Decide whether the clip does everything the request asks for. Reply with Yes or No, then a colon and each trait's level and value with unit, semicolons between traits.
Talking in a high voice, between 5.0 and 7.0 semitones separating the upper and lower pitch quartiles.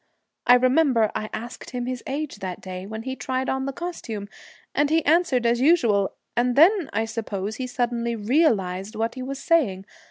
No: high, 245 Hz; average, 4.1 semitones